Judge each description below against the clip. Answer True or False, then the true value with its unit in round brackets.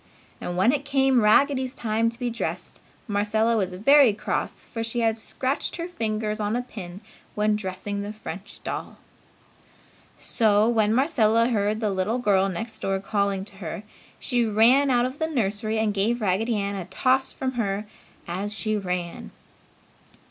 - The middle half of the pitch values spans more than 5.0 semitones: False (3.2 semitones)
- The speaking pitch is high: True (215 Hz)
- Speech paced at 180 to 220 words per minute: False (165 wpm)